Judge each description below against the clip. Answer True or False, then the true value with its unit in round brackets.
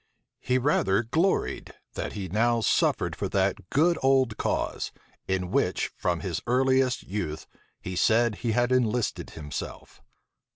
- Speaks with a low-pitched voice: True (115 Hz)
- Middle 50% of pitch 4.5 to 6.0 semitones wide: True (5.2 semitones)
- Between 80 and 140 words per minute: True (135 wpm)